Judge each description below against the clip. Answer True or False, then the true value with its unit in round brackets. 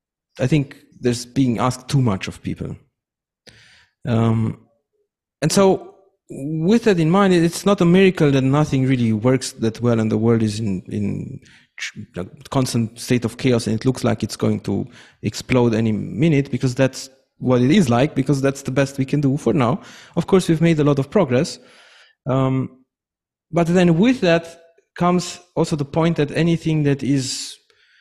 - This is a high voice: False (135 Hz)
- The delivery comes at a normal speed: True (180 wpm)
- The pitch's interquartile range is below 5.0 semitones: False (5.5 semitones)